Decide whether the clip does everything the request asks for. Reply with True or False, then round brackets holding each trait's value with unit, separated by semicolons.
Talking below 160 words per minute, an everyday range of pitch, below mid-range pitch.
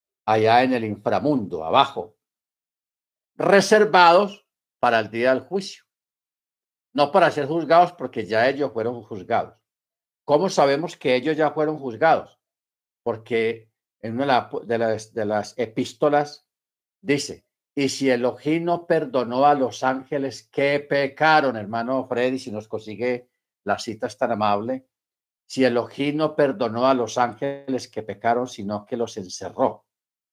True (130 wpm; 4.3 semitones; 130 Hz)